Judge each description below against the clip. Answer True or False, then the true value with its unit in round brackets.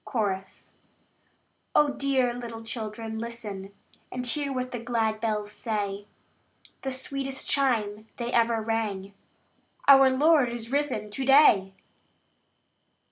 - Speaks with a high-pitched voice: True (235 Hz)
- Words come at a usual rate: False (115 wpm)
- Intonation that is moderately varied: True (3.7 semitones)